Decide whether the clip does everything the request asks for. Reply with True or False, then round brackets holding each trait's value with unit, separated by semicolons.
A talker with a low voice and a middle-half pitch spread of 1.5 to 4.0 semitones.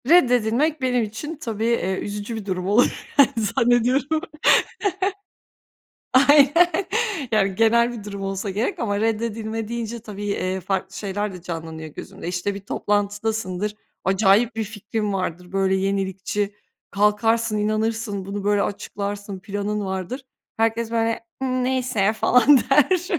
False (210 Hz; 3.0 semitones)